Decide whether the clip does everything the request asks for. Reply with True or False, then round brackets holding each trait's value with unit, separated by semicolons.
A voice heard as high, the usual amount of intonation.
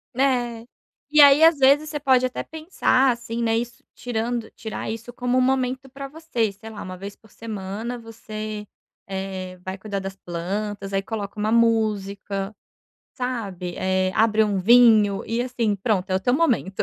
True (225 Hz; 3.9 semitones)